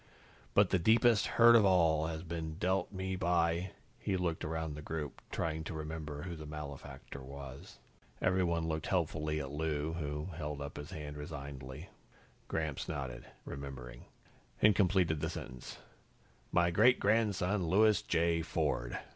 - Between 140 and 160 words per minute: Yes, average, 150 wpm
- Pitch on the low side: Yes, very low, 80 Hz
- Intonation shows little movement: No, average, 3.6 semitones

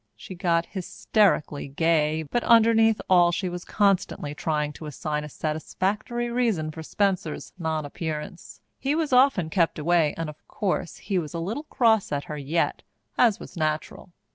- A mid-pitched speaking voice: Yes, medium, 170 Hz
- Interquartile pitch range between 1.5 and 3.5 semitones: No, average, 5.3 semitones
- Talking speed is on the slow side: No, average, 160 wpm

